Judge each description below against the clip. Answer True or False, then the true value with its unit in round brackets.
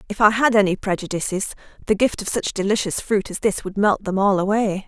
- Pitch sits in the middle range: False (200 Hz)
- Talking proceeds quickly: True (220 wpm)